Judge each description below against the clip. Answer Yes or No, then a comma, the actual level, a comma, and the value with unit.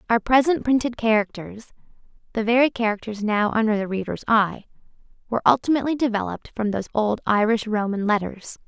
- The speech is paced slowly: Yes, slow, 130 wpm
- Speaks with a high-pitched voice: Yes, high, 220 Hz